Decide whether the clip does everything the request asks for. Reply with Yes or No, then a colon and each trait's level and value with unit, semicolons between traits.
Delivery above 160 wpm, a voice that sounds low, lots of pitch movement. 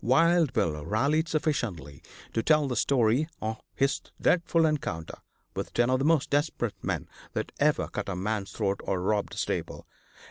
Yes: average, 170 wpm; low, 125 Hz; wide, 6.9 semitones